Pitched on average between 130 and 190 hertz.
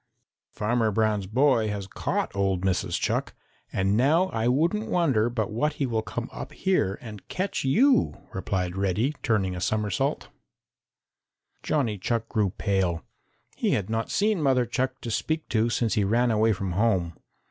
No: low, 110 Hz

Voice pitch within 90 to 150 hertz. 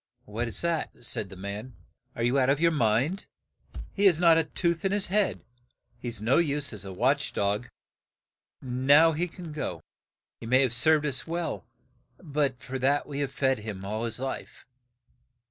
Yes: low, 135 Hz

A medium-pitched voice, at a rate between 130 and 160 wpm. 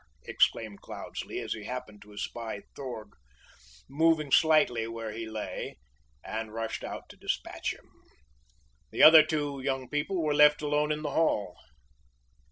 No: low, 130 Hz; average, 145 wpm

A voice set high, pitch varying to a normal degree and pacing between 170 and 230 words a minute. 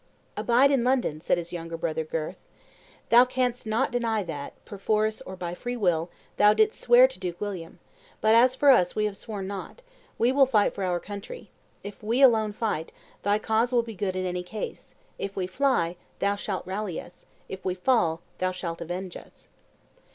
Yes: high, 205 Hz; average, 4.9 semitones; average, 190 wpm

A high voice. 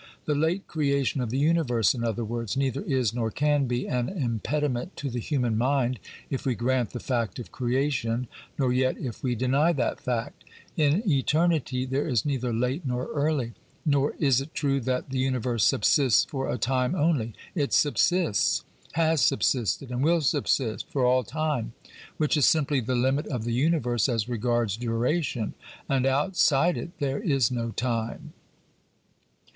No: low, 130 Hz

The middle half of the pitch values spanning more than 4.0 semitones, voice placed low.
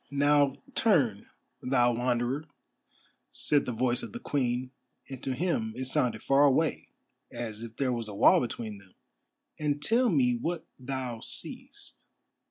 No: average, 3.3 semitones; low, 130 Hz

